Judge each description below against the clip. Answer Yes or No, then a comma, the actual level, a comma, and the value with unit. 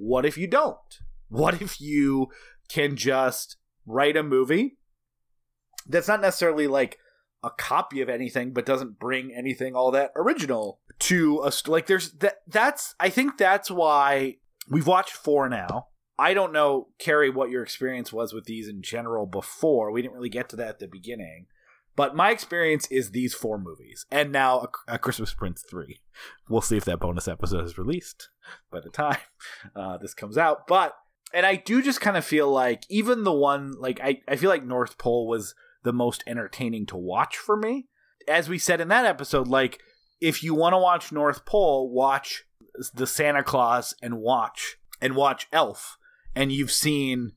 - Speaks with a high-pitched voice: No, low, 135 Hz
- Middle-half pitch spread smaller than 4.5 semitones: No, average, 4.9 semitones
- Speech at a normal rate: Yes, average, 185 wpm